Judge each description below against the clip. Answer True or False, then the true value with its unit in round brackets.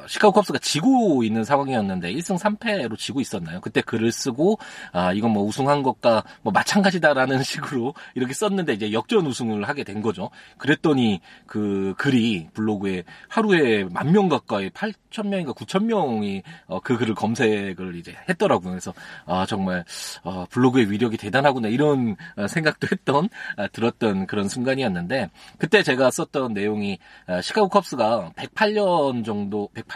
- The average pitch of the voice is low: True (130 Hz)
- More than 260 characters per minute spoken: True (325 characters per minute)